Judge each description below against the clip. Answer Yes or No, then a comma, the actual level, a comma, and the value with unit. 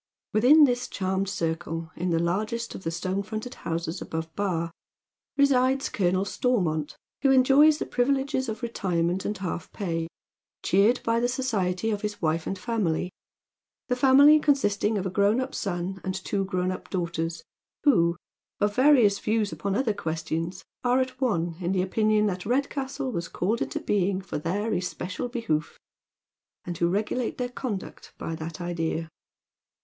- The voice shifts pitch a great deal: Yes, wide, 6.0 semitones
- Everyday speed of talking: Yes, average, 165 wpm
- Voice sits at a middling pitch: No, high, 200 Hz